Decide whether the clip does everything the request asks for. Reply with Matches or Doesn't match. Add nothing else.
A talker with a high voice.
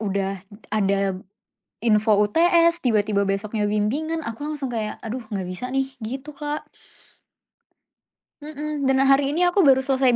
Matches